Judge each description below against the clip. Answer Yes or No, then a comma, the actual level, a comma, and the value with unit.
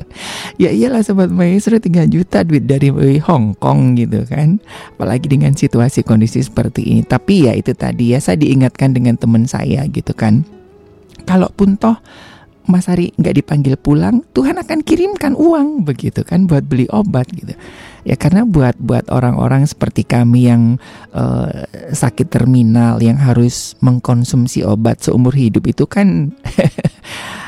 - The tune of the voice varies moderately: No, wide, 7.0 semitones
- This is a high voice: No, low, 135 Hz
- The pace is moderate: No, fast, 145 wpm